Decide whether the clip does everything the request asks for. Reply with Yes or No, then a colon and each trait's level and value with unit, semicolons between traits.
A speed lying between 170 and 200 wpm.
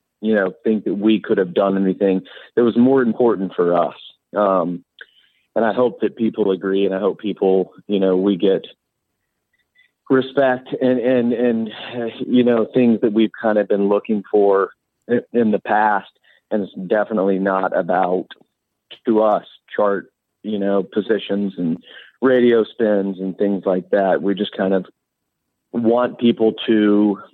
No: average, 160 wpm